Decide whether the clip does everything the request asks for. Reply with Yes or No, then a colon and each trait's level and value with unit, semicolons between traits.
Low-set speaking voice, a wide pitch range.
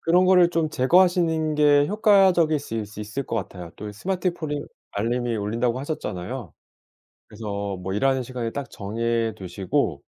Yes: low, 125 Hz; wide, 7.2 semitones